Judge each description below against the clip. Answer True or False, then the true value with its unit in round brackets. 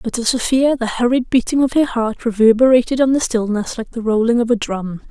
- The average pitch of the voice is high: True (235 Hz)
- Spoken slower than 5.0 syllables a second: False (5.6 syllables/s)